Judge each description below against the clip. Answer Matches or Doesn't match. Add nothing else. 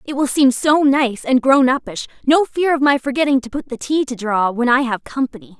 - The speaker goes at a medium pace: Doesn't match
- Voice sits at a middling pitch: Doesn't match